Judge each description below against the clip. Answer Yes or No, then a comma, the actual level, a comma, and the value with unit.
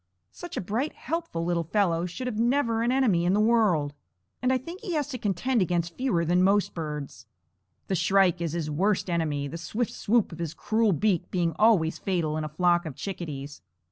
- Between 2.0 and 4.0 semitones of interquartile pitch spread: No, wide, 5.4 semitones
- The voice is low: No, medium, 180 Hz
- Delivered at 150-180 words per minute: No, fast, 205 wpm